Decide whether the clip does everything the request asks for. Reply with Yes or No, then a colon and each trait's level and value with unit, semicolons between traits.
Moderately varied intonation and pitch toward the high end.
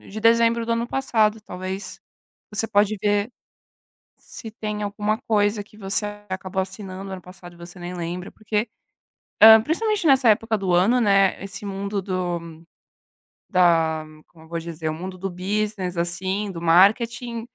Yes: average, 3.2 semitones; high, 200 Hz